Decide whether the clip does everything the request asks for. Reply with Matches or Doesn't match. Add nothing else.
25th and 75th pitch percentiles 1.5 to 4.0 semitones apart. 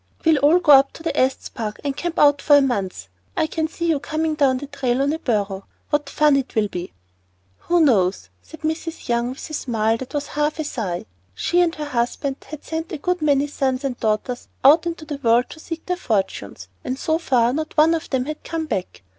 Doesn't match